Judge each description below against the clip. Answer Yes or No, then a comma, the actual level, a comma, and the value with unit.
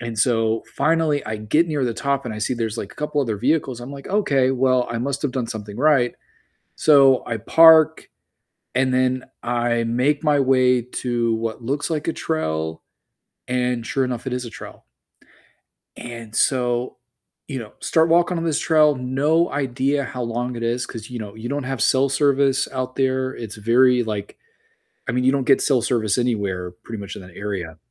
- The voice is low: Yes, low, 125 Hz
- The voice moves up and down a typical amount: Yes, average, 3.3 semitones